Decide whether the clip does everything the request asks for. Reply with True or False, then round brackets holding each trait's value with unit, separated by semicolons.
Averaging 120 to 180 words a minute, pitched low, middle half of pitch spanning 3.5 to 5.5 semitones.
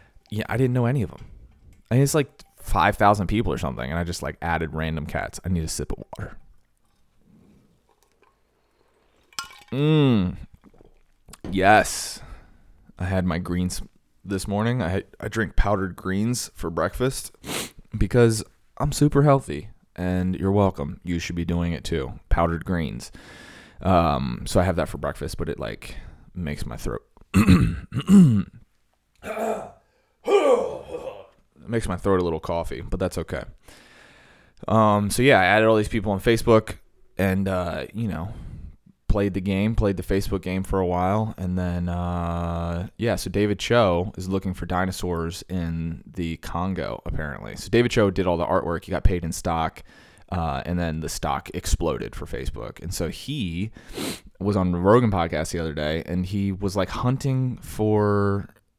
True (165 wpm; 95 Hz; 4.1 semitones)